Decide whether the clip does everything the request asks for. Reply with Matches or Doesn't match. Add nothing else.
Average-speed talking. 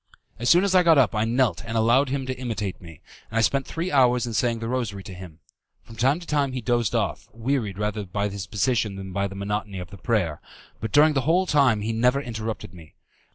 Doesn't match